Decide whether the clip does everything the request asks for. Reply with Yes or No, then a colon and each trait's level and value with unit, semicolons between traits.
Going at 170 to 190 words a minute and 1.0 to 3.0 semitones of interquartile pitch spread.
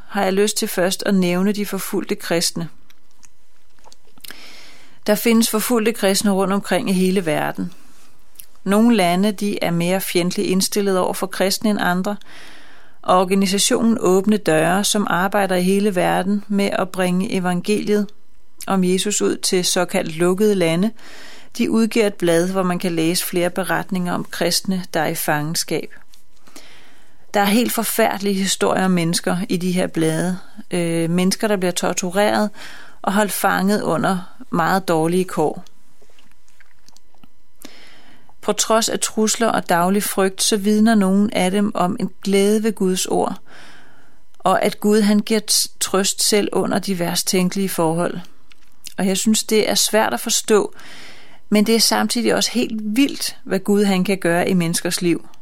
No: average, 155 wpm; average, 2.7 semitones